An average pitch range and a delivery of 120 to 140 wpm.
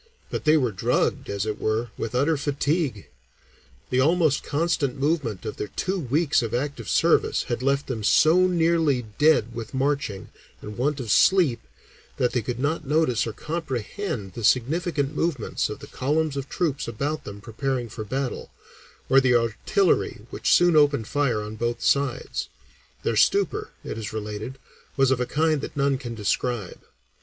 No: average, 4.8 semitones; average, 165 wpm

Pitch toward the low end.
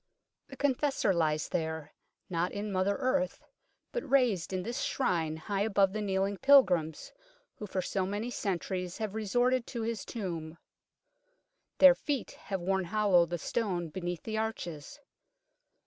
No: high, 195 Hz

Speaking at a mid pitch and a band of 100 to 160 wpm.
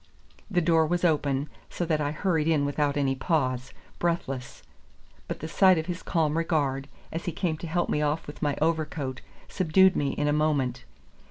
No: medium, 155 Hz; average, 185 wpm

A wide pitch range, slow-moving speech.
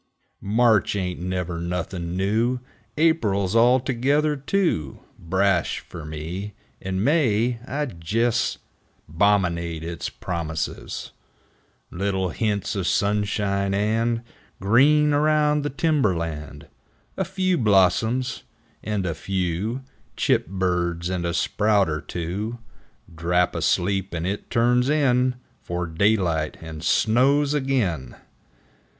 Yes: wide, 5.9 semitones; slow, 110 wpm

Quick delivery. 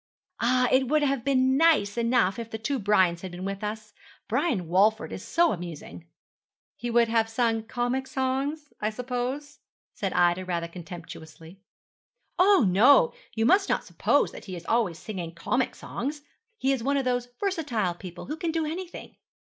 No: average, 170 wpm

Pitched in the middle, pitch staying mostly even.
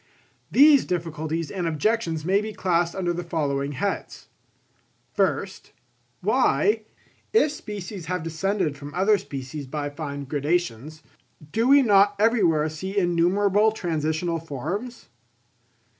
No: medium, 175 Hz; average, 4.8 semitones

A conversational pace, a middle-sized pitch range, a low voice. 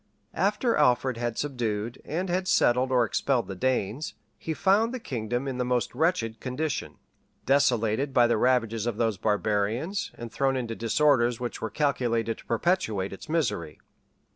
Yes: average, 160 wpm; average, 4.1 semitones; low, 125 Hz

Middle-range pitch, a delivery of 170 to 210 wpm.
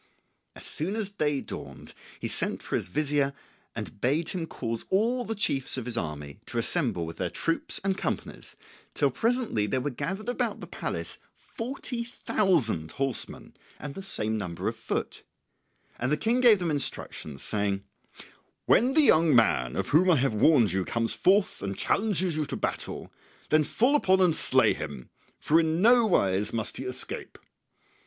Yes: medium, 150 Hz; average, 175 wpm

